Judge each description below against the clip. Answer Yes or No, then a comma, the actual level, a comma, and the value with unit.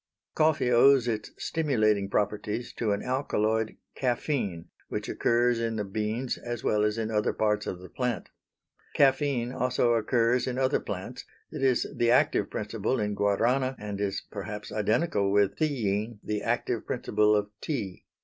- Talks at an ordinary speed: Yes, average, 155 wpm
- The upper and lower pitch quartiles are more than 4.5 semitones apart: No, average, 3.2 semitones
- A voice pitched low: Yes, low, 110 Hz